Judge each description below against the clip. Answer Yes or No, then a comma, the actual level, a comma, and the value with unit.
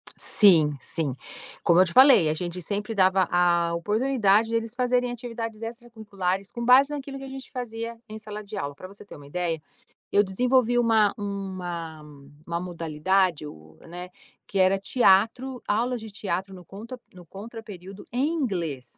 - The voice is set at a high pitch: Yes, high, 200 Hz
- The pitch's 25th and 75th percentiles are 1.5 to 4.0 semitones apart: No, average, 4.7 semitones